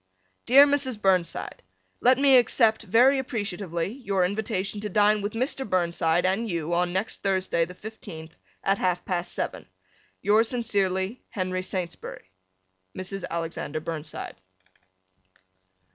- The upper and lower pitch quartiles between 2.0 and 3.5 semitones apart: No, average, 4.1 semitones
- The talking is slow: Yes, slow, 125 wpm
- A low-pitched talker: No, high, 195 Hz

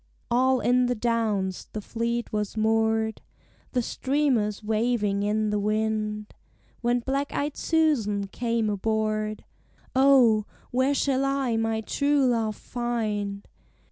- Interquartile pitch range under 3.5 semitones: Yes, average, 2.9 semitones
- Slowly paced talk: Yes, slow, 120 wpm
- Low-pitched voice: No, high, 225 Hz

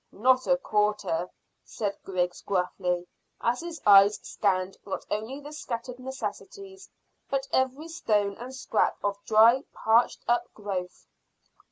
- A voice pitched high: Yes, high, 220 Hz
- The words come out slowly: Yes, slow, 130 wpm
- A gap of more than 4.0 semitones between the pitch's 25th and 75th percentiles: Yes, average, 4.8 semitones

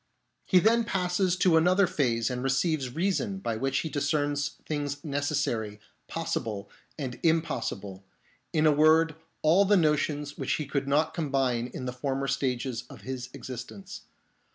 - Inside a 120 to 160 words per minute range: Yes, average, 150 wpm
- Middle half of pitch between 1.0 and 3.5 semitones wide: No, average, 4.3 semitones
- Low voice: No, medium, 145 Hz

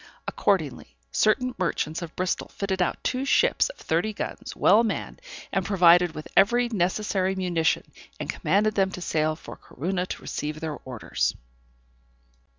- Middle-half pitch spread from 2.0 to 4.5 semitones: Yes, average, 4.0 semitones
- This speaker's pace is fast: No, average, 150 wpm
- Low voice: No, medium, 185 Hz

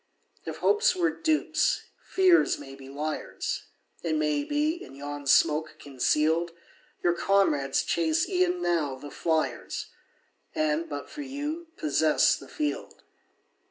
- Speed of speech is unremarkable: No, slow, 115 wpm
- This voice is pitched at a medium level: Yes, medium, 170 Hz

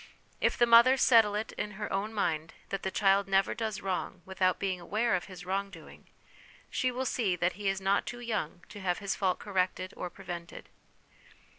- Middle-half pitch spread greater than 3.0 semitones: No, narrow, 2.5 semitones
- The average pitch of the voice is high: Yes, high, 195 Hz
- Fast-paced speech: No, average, 195 wpm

